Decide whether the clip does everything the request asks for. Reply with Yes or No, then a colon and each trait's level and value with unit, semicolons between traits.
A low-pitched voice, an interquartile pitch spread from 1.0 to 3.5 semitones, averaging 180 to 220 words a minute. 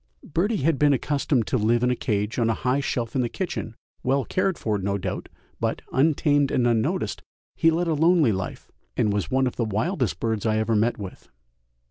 No: low, 125 Hz; average, 4.9 semitones; fast, 205 wpm